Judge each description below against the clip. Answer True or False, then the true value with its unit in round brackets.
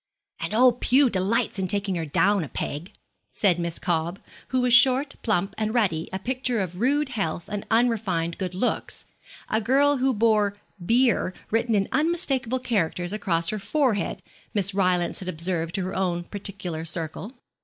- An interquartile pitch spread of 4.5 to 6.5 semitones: True (5.5 semitones)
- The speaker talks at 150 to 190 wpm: True (165 wpm)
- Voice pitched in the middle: False (200 Hz)